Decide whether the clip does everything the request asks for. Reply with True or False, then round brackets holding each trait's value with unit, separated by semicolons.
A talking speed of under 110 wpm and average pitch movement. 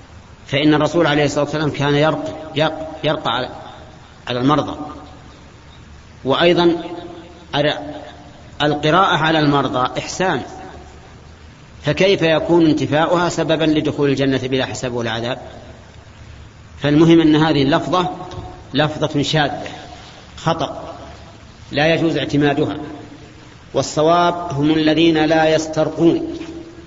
True (90 wpm; 3.1 semitones)